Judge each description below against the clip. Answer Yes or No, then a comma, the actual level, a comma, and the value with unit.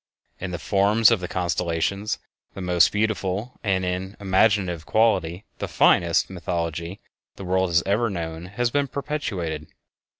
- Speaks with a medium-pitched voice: No, very low, 95 Hz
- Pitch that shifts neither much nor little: Yes, average, 3.3 semitones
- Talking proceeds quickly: No, average, 145 wpm